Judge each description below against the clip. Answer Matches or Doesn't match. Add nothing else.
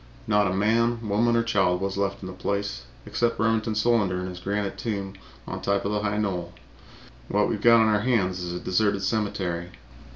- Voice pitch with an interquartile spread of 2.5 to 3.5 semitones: Matches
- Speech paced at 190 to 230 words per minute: Matches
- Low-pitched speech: Matches